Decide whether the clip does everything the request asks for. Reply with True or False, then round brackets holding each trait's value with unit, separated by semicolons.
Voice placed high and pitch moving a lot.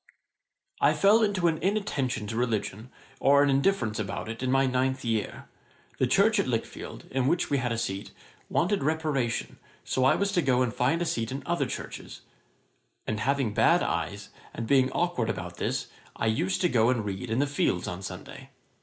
False (130 Hz; 6.0 semitones)